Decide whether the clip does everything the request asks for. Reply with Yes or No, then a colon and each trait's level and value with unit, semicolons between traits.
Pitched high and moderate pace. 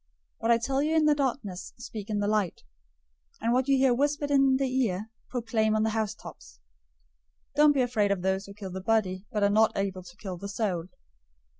No: high, 220 Hz; fast, 215 wpm